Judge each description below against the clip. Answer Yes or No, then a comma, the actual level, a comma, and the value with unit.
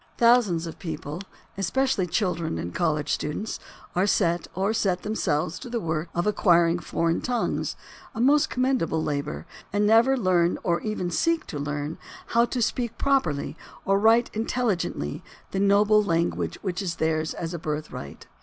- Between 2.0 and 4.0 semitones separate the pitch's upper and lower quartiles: No, wide, 5.6 semitones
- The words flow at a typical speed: Yes, average, 160 wpm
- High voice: No, medium, 180 Hz